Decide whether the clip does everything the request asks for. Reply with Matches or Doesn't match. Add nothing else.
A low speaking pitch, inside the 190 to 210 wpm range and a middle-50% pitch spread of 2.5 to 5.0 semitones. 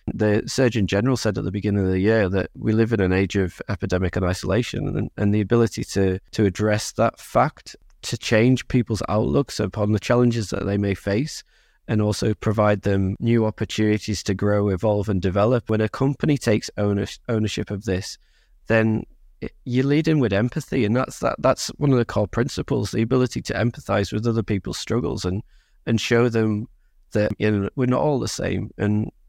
Matches